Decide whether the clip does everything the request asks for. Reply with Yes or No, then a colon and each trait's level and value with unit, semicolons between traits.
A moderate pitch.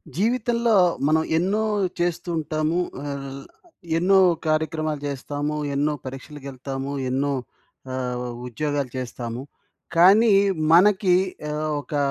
Yes: medium, 150 Hz